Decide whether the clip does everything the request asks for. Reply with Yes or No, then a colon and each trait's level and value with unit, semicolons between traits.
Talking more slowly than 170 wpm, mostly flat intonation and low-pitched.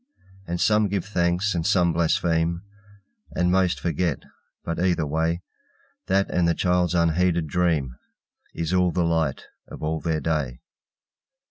Yes: average, 140 wpm; narrow, 1.7 semitones; very low, 85 Hz